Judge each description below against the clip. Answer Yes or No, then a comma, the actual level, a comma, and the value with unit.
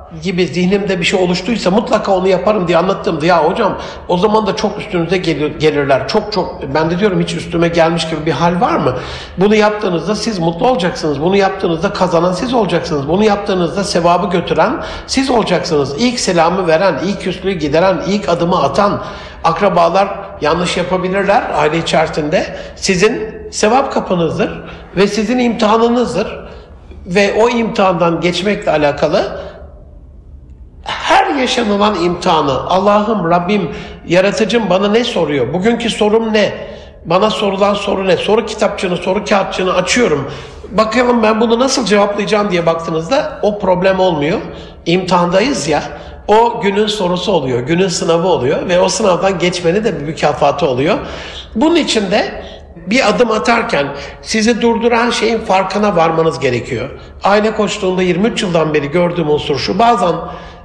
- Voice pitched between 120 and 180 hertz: No, high, 190 Hz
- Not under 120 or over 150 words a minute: Yes, fast, 140 wpm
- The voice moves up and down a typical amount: Yes, average, 4.0 semitones